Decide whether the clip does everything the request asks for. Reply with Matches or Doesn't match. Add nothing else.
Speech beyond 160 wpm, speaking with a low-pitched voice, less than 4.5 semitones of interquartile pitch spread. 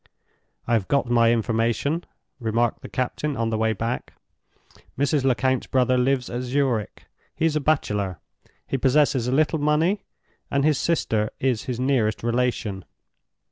Doesn't match